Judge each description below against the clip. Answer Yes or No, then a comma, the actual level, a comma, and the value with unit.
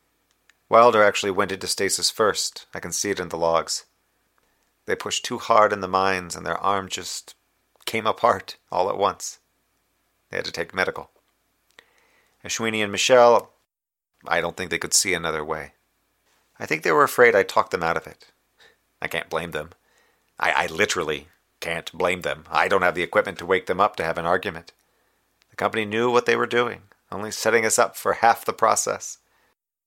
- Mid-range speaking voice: No, low, 105 Hz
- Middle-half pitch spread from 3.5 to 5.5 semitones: Yes, average, 4.5 semitones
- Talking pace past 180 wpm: Yes, average, 190 wpm